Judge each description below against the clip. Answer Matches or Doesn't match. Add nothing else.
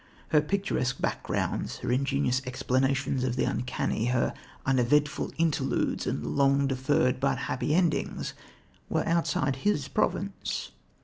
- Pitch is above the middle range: Doesn't match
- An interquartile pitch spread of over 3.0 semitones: Doesn't match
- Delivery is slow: Matches